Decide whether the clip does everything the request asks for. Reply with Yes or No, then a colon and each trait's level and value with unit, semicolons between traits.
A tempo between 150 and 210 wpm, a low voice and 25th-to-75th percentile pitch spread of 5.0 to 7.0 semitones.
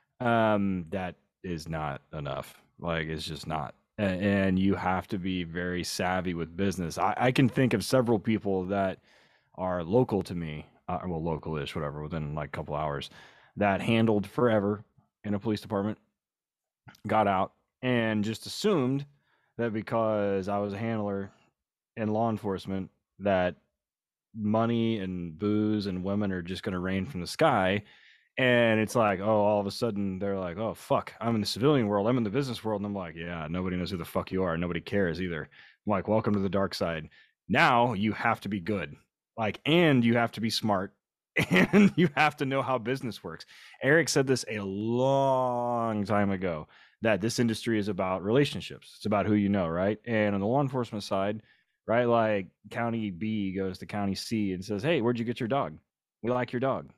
No: average, 195 wpm; low, 105 Hz; average, 3.8 semitones